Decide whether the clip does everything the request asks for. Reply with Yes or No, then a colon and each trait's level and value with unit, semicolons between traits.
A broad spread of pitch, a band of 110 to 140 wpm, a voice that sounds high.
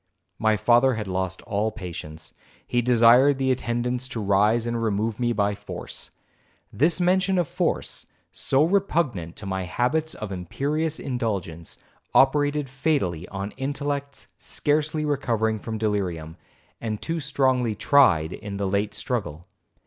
No: wide, 5.8 semitones; slow, 135 wpm; low, 120 Hz